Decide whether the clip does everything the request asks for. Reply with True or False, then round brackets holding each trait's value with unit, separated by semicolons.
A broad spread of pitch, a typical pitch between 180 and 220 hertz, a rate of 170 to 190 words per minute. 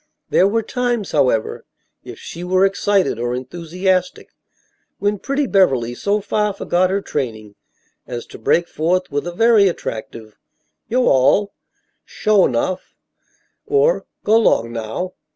False (7.9 semitones; 185 Hz; 135 wpm)